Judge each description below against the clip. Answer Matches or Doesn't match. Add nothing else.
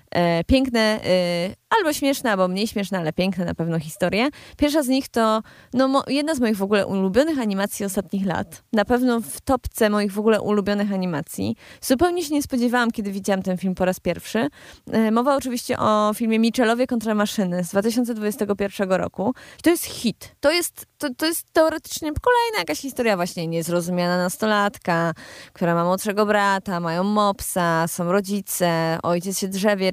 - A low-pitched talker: Doesn't match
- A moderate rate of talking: Doesn't match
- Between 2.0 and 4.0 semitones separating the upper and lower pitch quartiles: Doesn't match